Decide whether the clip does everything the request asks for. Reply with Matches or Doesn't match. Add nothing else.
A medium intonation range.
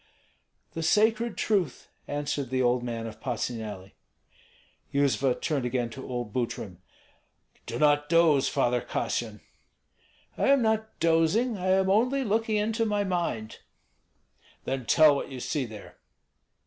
Doesn't match